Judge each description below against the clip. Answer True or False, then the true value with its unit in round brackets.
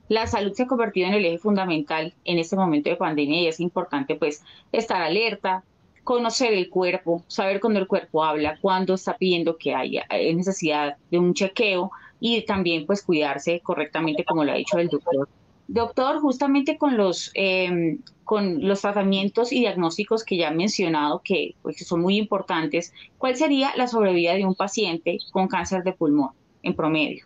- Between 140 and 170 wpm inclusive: False (180 wpm)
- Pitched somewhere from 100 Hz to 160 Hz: False (185 Hz)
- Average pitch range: True (4.1 semitones)